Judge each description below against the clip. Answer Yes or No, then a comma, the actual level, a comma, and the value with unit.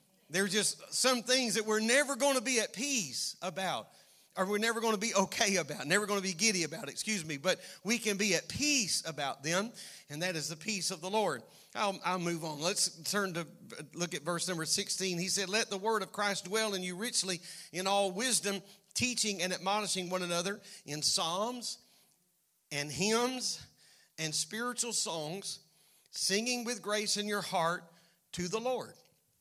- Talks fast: No, average, 190 wpm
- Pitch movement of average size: Yes, average, 3.5 semitones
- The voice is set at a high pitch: Yes, high, 195 Hz